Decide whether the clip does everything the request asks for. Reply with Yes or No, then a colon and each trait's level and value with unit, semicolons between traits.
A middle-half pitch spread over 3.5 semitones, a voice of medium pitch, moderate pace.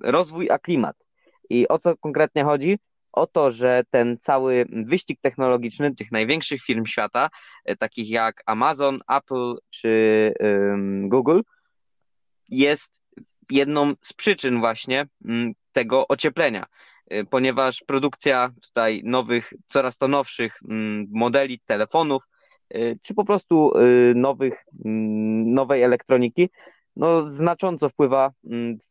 No: average, 3.9 semitones; low, 130 Hz; average, 120 wpm